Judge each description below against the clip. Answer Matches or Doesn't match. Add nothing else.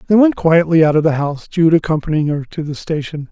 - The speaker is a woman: Doesn't match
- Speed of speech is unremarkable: Doesn't match